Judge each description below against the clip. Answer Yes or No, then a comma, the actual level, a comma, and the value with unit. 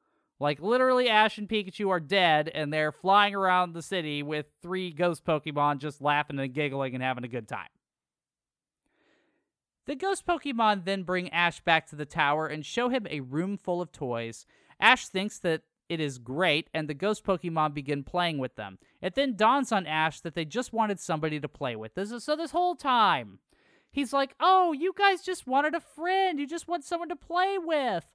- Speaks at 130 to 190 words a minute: No, average, 200 wpm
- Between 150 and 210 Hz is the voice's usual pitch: Yes, medium, 185 Hz